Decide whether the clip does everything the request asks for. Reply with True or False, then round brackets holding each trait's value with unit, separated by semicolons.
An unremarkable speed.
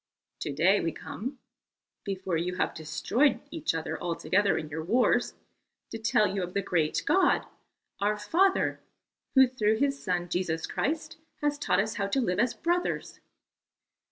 True (155 wpm)